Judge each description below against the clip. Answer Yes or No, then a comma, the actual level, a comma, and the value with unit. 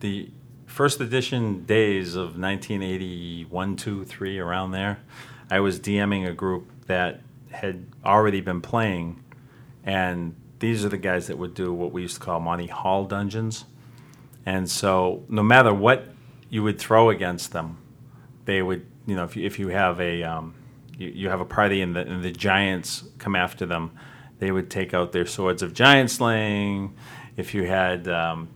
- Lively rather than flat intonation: No, average, 4.3 semitones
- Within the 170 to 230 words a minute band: Yes, average, 175 wpm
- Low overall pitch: Yes, very low, 95 Hz